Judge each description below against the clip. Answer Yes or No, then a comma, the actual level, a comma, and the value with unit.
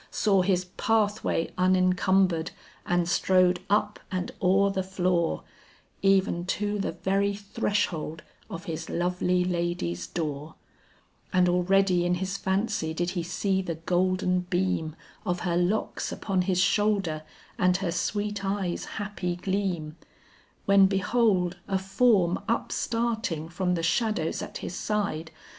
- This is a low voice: No, medium, 185 Hz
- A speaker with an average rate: No, slow, 130 wpm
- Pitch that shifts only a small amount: Yes, narrow, 2.2 semitones